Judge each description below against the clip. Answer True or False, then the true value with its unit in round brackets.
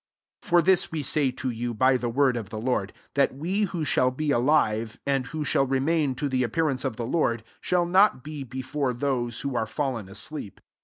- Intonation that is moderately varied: True (4.1 semitones)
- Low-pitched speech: True (130 Hz)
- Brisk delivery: True (210 wpm)